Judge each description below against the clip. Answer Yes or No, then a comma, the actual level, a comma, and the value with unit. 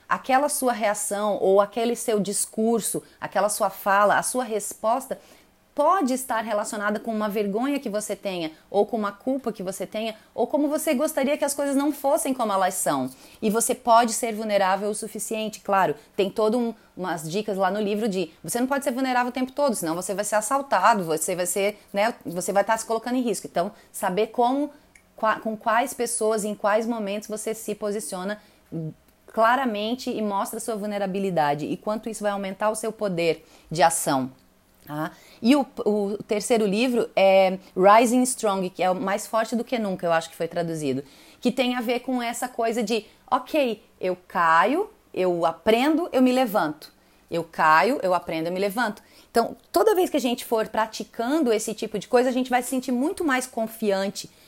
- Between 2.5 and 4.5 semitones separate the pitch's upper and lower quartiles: Yes, average, 3.9 semitones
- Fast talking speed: Yes, fast, 190 wpm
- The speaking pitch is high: Yes, high, 215 Hz